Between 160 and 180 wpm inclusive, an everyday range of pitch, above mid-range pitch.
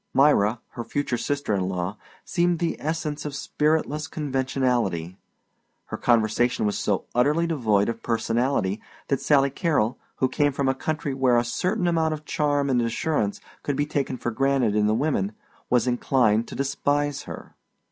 No: average, 165 wpm; average, 4.3 semitones; low, 135 Hz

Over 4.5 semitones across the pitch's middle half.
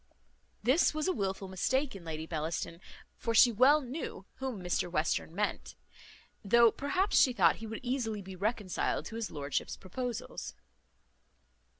Yes: wide, 5.5 semitones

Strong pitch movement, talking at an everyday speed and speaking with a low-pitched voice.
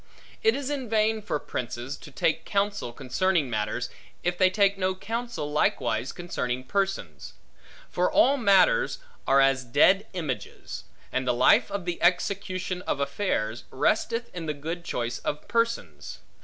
No: wide, 7.7 semitones; average, 150 wpm; medium, 175 Hz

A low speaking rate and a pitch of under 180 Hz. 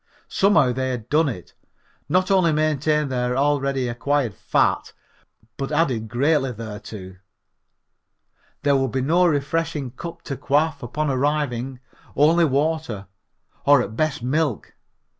Yes: slow, 125 wpm; medium, 140 Hz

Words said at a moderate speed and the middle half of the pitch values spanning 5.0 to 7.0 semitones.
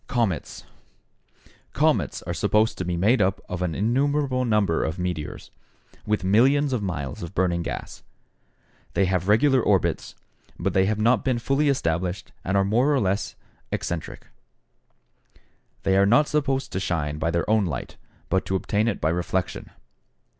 Yes: average, 160 wpm; average, 5.3 semitones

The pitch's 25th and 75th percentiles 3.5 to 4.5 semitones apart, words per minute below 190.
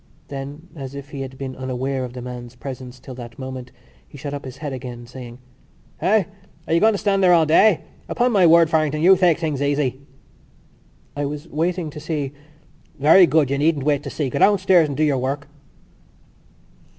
No: average, 3.8 semitones; average, 200 wpm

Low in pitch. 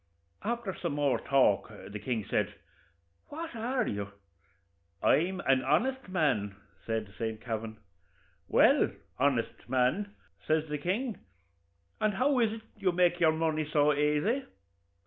No: medium, 155 Hz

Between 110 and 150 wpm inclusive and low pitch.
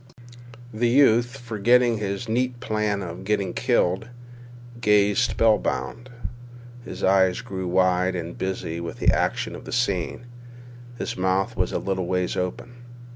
Yes: average, 140 wpm; low, 100 Hz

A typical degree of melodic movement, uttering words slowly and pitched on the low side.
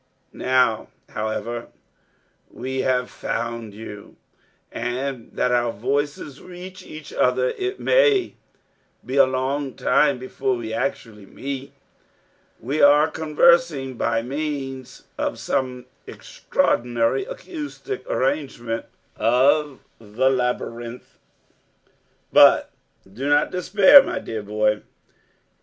Yes: average, 3.9 semitones; slow, 105 wpm; low, 130 Hz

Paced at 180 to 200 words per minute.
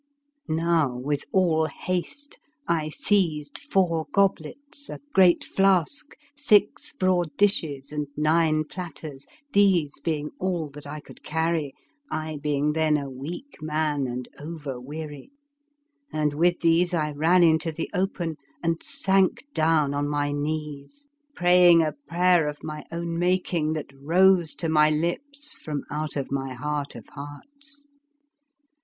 No: slow, 135 wpm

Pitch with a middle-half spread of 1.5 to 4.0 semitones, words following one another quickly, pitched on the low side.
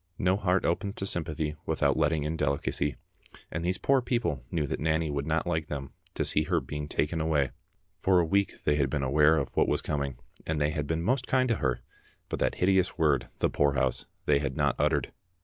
Yes: average, 3.4 semitones; fast, 215 wpm; very low, 80 Hz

